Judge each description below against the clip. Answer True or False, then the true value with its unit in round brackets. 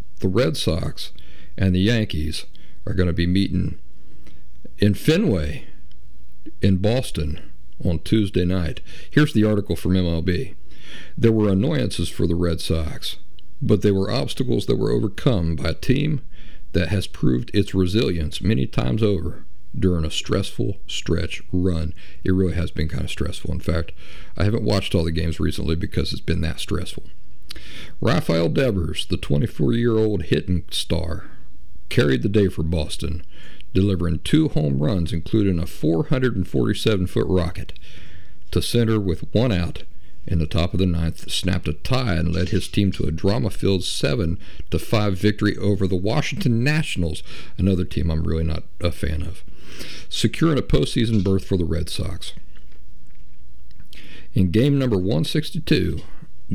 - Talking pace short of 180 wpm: True (150 wpm)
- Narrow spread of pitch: False (4.1 semitones)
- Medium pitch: False (90 Hz)